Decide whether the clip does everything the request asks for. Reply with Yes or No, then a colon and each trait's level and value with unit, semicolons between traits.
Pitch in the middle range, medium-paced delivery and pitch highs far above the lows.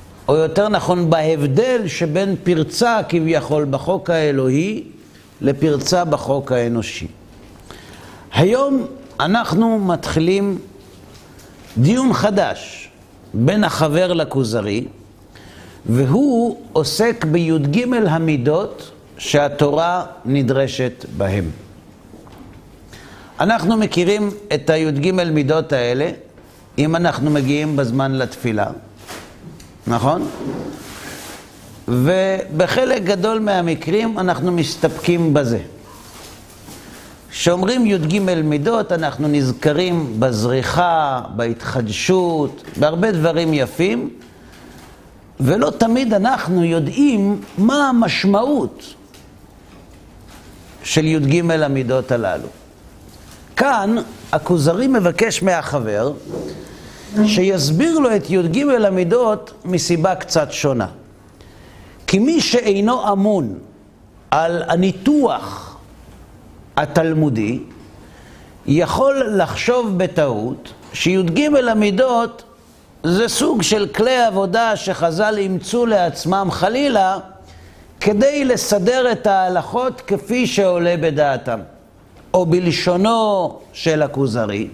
No: medium, 165 Hz; slow, 75 wpm; wide, 7.9 semitones